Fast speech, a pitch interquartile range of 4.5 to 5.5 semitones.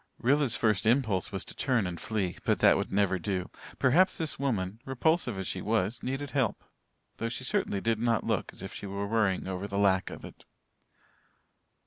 No: average, 190 wpm; average, 5.1 semitones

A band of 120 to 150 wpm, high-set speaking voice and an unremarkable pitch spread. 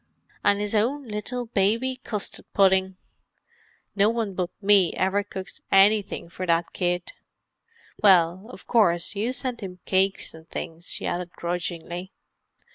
Yes: slow, 135 wpm; high, 195 Hz; average, 3.1 semitones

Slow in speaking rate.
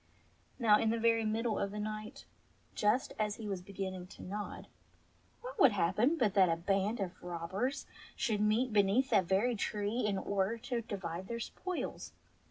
No: average, 175 wpm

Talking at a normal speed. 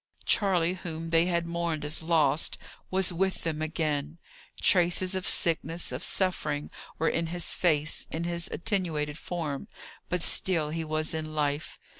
Yes: average, 150 wpm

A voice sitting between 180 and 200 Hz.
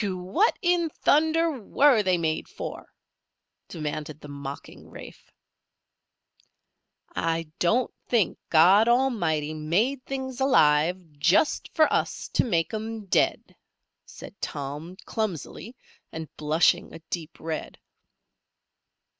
Yes: medium, 185 Hz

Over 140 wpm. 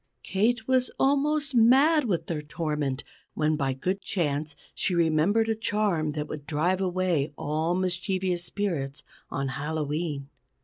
No: slow, 135 wpm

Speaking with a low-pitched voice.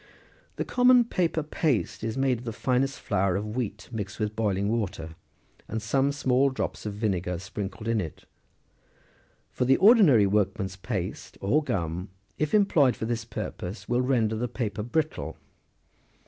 Yes: low, 110 Hz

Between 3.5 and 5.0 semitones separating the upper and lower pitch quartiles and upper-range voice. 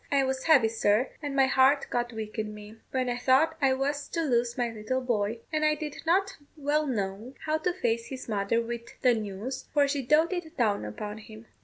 Yes: average, 4.6 semitones; very high, 255 Hz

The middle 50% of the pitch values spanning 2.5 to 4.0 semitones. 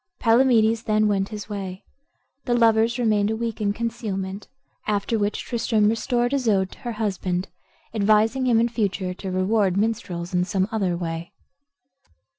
Yes: average, 2.9 semitones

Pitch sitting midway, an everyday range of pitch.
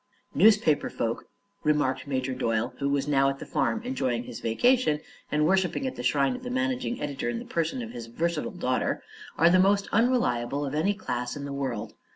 No: medium, 150 Hz; wide, 7.8 semitones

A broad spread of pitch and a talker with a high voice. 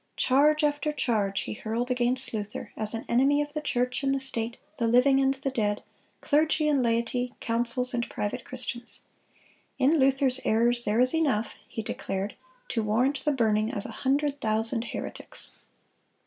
No: average, 3.2 semitones; very high, 250 Hz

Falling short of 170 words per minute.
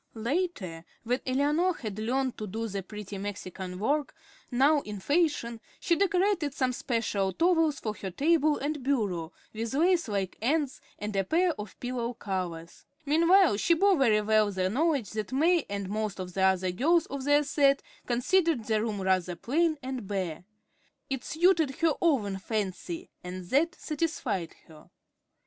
Yes: average, 160 wpm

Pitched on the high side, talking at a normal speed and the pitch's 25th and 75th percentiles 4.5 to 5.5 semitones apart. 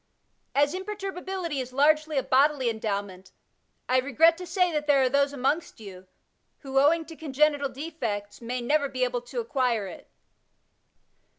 No: very high, 280 Hz; average, 155 wpm; average, 4.1 semitones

